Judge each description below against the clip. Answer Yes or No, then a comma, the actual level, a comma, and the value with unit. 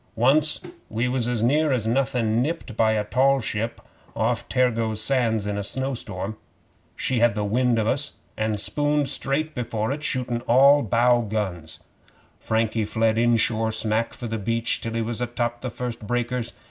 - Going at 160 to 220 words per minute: Yes, average, 170 wpm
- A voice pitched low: Yes, low, 115 Hz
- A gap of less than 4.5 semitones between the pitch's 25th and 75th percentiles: Yes, narrow, 2.6 semitones